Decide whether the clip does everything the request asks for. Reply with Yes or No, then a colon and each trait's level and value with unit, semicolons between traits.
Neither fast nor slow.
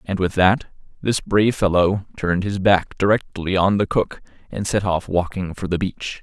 Yes: average, 195 wpm